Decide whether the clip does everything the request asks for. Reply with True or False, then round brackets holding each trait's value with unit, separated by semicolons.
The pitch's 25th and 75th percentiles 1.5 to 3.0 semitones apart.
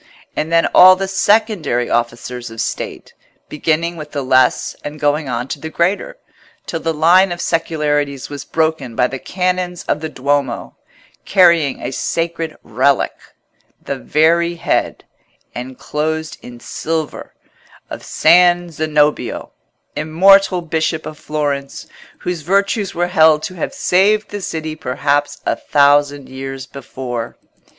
False (3.5 semitones)